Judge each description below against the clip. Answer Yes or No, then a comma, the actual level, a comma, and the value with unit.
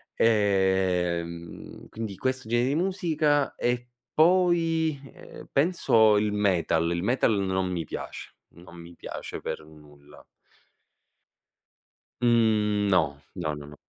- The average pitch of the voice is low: Yes, low, 105 Hz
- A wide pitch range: Yes, wide, 7.2 semitones